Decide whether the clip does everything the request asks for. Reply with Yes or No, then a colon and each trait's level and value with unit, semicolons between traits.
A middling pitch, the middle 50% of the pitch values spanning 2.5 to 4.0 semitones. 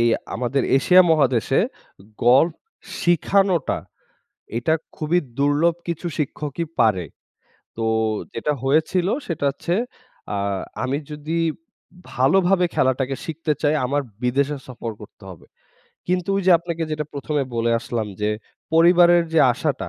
No: medium, 150 Hz; average, 4.7 semitones